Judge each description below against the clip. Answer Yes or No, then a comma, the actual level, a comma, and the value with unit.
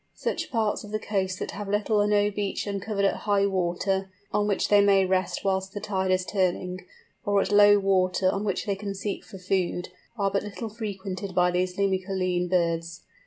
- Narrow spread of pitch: Yes, narrow, 1.8 semitones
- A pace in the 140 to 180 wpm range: No, average, 200 wpm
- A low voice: No, high, 195 Hz